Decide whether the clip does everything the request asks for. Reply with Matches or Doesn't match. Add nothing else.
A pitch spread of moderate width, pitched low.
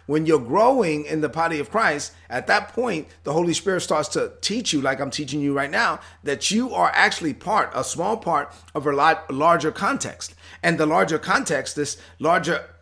Doesn't match